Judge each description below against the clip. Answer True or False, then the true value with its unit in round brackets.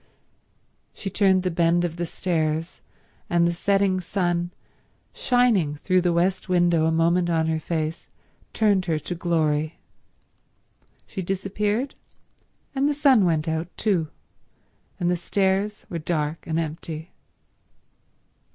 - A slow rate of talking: True (130 wpm)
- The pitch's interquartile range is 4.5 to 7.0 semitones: False (3.0 semitones)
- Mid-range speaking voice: True (175 Hz)